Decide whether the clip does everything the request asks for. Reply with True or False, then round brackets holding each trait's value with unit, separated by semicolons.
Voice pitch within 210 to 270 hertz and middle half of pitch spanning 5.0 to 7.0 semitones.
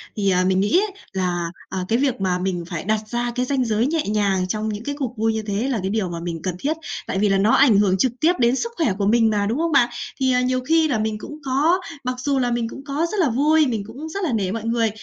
True (230 Hz; 5.4 semitones)